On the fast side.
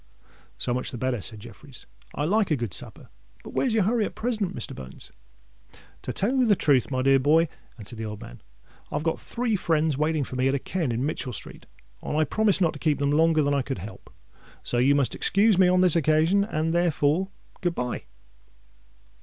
Yes: fast, 215 wpm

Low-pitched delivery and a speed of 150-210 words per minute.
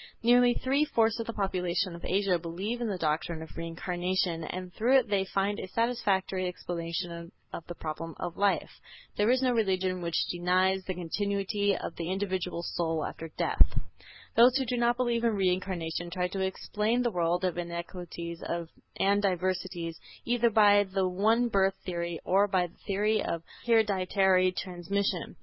No: high, 190 Hz; average, 165 wpm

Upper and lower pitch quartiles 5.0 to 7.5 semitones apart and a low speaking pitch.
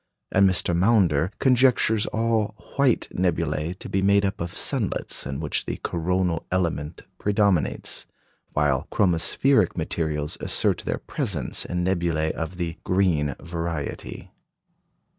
No: average, 3.5 semitones; very low, 90 Hz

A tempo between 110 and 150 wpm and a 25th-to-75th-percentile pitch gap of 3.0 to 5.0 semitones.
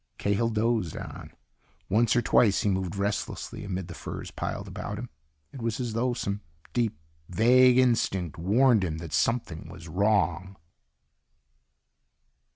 Yes: average, 140 wpm; average, 4.2 semitones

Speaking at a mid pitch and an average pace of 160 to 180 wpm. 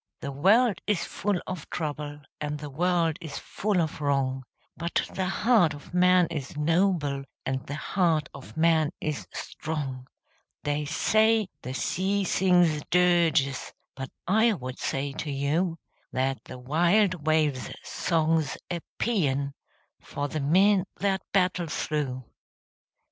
No: medium, 160 Hz; slow, 135 wpm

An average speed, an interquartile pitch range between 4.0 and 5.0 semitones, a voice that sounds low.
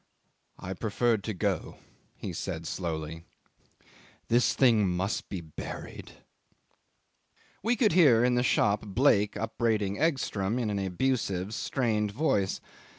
No: slow, 120 wpm; average, 4.3 semitones; low, 105 Hz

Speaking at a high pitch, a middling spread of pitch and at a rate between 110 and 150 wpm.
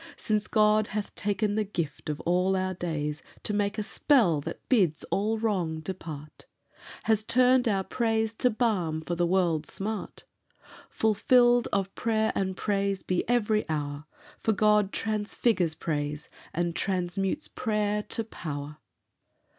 Yes: high, 200 Hz; average, 4.1 semitones; average, 140 wpm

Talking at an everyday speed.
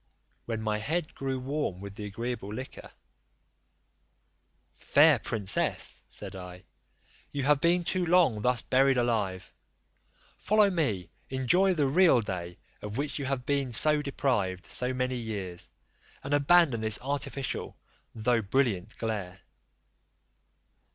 No: slow, 125 wpm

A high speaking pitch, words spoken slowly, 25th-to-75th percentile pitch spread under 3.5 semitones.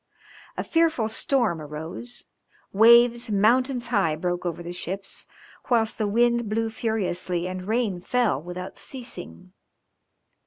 No: high, 215 Hz; slow, 120 wpm; average, 5.0 semitones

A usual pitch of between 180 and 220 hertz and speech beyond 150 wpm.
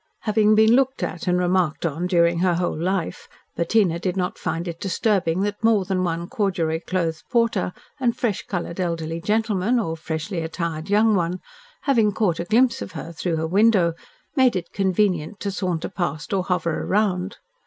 Yes: medium, 185 Hz; average, 175 wpm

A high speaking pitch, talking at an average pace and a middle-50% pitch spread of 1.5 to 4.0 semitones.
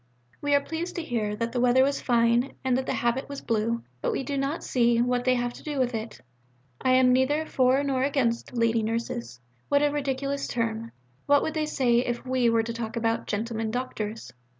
No: high, 245 Hz; fast, 215 wpm; average, 3.0 semitones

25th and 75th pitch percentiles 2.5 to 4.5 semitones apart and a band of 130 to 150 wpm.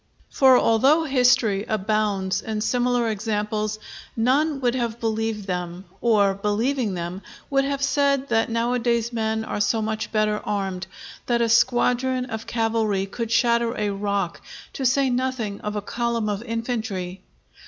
Yes: average, 2.9 semitones; average, 145 wpm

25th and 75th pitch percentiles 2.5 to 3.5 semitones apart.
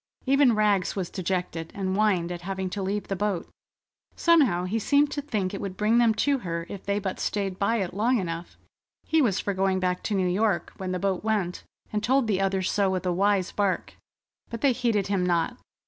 Yes: average, 2.8 semitones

